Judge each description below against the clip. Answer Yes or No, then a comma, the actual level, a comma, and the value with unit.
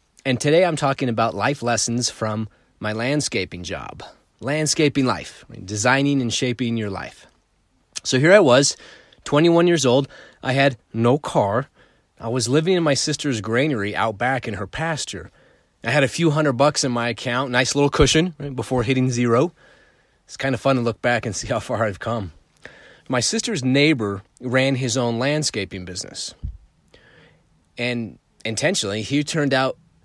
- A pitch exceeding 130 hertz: No, low, 125 Hz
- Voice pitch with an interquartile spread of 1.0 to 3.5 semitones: No, average, 4.0 semitones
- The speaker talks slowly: No, average, 165 wpm